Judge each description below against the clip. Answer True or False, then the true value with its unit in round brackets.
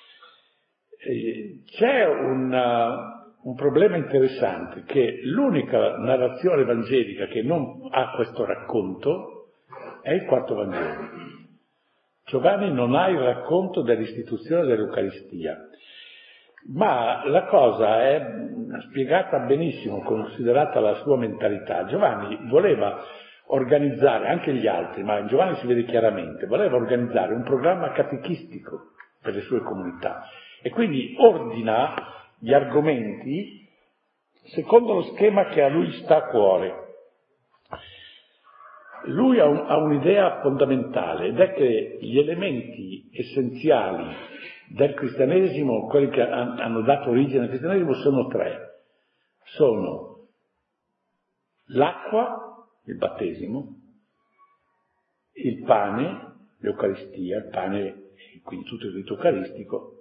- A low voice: False (150 Hz)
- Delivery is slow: True (105 wpm)